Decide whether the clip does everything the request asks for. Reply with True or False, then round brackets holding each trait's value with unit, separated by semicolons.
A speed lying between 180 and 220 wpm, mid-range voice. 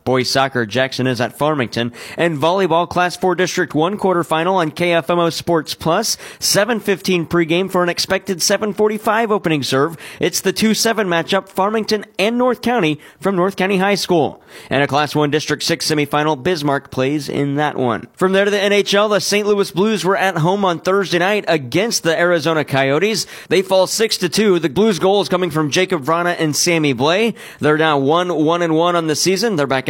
True (190 wpm; 175 Hz)